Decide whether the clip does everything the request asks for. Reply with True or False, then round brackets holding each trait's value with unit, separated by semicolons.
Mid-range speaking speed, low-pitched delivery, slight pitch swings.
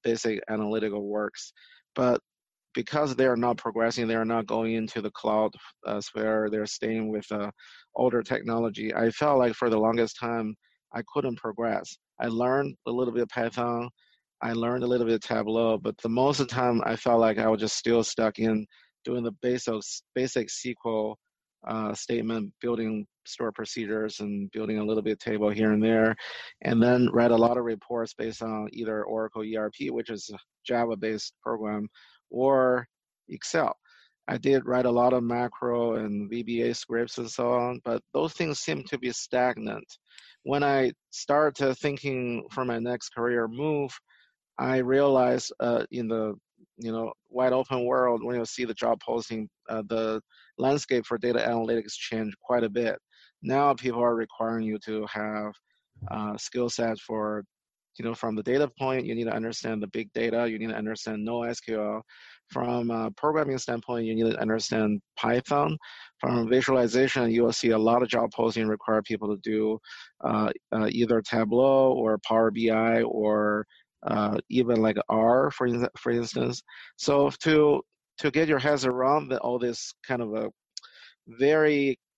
True (170 wpm; 115 Hz; 2.1 semitones)